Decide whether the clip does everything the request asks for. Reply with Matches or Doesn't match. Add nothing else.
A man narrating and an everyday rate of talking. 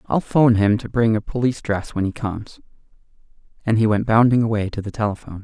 Doesn't match